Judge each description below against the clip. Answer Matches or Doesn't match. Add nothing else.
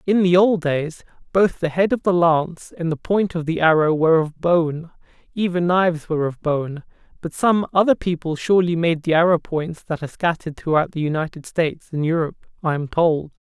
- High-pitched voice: Doesn't match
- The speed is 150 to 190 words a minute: Doesn't match